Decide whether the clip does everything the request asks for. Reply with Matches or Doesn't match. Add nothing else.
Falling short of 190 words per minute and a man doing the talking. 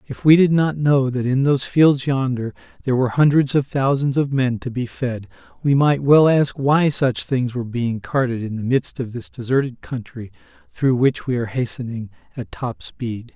Doesn't match